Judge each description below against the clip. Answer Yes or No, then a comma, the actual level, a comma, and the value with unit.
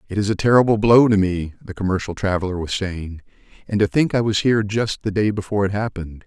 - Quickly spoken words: Yes, fast, 230 wpm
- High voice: No, low, 100 Hz